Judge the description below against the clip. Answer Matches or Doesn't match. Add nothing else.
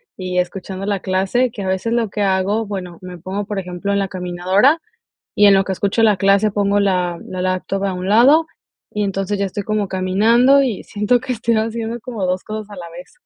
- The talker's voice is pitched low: Doesn't match